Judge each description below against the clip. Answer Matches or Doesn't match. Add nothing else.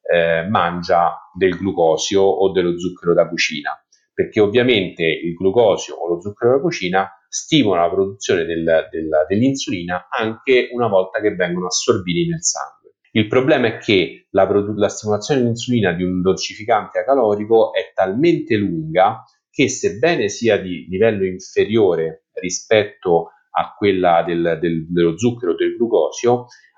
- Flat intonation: Doesn't match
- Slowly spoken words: Doesn't match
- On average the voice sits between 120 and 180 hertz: Doesn't match